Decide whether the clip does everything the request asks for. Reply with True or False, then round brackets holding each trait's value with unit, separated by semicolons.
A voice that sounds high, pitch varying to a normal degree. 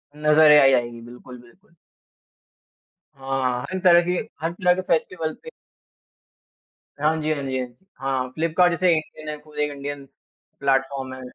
False (150 Hz; 3.6 semitones)